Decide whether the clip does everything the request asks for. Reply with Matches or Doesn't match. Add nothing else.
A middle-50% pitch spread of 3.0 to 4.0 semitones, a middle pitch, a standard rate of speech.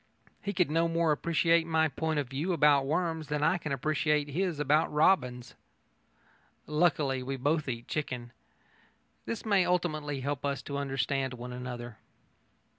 Matches